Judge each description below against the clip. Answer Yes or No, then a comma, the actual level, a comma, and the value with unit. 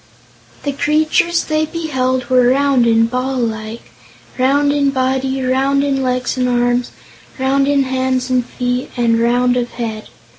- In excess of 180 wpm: No, average, 150 wpm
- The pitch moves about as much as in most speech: No, narrow, 2.1 semitones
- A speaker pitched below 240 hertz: No, very high, 260 Hz